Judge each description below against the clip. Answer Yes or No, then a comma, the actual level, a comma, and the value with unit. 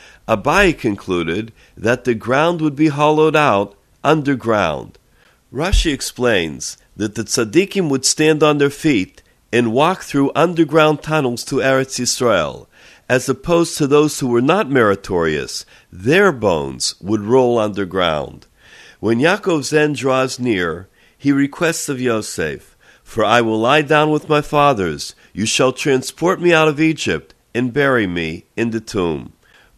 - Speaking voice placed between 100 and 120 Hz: No, low, 135 Hz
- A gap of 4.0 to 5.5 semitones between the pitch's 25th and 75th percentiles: Yes, average, 5.1 semitones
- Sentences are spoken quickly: No, average, 145 wpm